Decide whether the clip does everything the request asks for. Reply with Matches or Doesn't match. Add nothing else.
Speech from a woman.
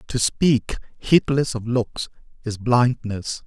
Doesn't match